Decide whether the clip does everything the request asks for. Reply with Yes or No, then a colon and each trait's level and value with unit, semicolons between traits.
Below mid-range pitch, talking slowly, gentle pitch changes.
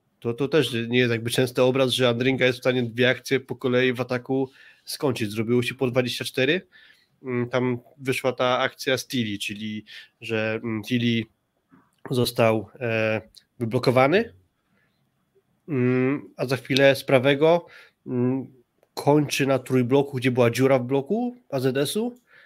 No: low, 130 Hz; average, 130 wpm; narrow, 2.0 semitones